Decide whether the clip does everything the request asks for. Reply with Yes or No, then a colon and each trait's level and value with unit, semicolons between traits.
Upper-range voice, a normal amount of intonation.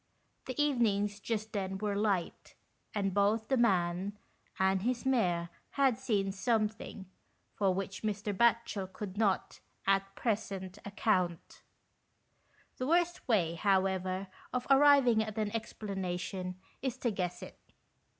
Yes: high, 205 Hz; average, 3.2 semitones